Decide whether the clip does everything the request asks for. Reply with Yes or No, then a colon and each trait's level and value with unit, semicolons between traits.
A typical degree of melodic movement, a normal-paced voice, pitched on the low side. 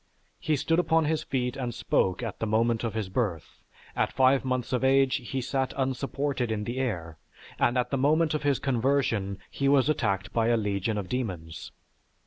Yes: average, 3.9 semitones; average, 190 wpm; low, 125 Hz